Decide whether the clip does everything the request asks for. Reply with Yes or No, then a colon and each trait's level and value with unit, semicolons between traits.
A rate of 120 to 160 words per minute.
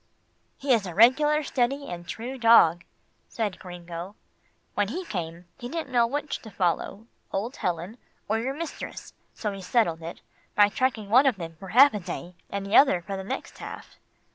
No: average, 185 wpm